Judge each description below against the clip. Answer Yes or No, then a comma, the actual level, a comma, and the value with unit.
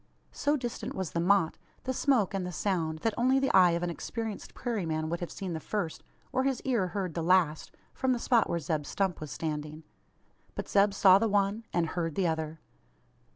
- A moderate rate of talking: No, fast, 210 wpm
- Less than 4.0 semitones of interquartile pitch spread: No, average, 5.2 semitones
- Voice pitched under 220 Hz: Yes, medium, 185 Hz